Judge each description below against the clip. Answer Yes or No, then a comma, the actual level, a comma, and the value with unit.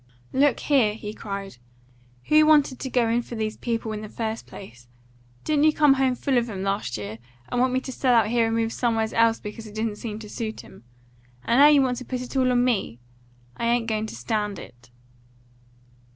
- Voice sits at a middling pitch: No, high, 230 Hz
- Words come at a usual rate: No, fast, 220 wpm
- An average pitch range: Yes, average, 3.2 semitones